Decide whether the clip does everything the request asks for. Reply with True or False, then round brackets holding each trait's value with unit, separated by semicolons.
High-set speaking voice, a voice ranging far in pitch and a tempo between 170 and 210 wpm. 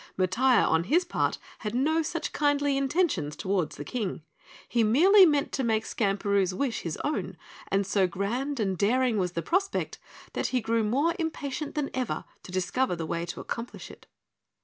True (235 Hz; 6.9 semitones; 175 wpm)